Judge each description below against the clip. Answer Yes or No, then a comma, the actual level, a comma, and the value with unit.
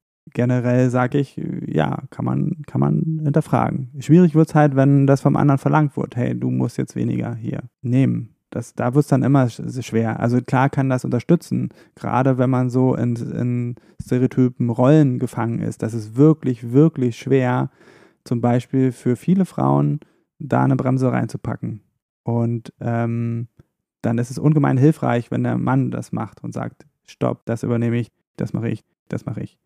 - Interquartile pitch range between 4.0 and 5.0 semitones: No, average, 3.4 semitones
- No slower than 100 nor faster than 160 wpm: No, average, 170 wpm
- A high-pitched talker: No, low, 125 Hz